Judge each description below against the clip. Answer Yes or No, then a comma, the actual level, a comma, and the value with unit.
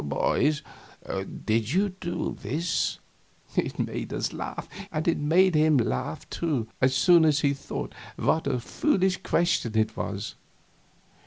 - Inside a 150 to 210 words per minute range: No, average, 140 wpm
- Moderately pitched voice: Yes, medium, 155 Hz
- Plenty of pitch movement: Yes, wide, 6.3 semitones